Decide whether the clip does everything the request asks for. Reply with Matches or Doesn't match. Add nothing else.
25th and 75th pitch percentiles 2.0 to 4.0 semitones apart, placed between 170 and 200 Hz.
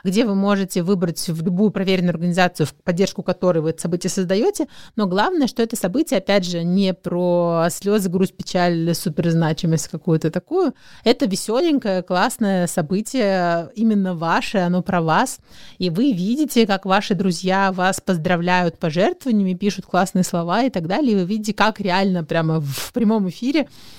Matches